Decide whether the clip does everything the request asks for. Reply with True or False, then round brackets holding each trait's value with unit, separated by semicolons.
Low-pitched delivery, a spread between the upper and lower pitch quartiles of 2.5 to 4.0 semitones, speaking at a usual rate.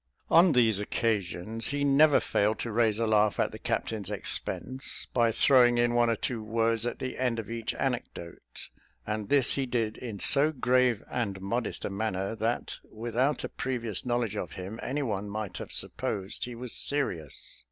True (115 Hz; 2.9 semitones; 175 wpm)